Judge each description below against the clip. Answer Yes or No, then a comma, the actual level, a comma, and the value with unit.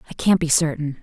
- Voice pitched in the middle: Yes, medium, 155 Hz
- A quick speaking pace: Yes, fast, 235 wpm